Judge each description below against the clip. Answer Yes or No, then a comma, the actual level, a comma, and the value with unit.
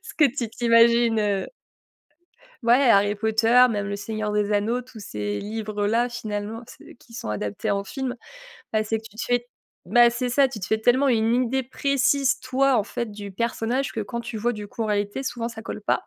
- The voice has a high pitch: Yes, high, 225 Hz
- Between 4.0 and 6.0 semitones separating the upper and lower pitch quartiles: No, average, 2.7 semitones